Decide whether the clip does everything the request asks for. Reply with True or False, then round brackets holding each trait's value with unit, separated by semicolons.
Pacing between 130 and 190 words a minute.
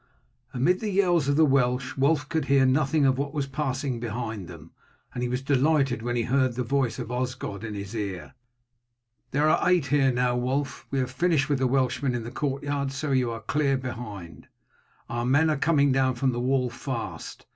False (200 wpm)